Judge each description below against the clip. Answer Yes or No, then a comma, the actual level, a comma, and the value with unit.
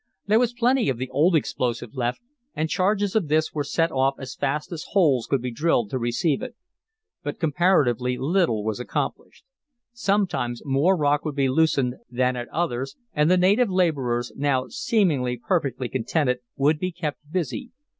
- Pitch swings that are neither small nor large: No, wide, 6.0 semitones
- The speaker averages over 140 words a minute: Yes, average, 170 wpm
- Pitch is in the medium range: Yes, medium, 145 Hz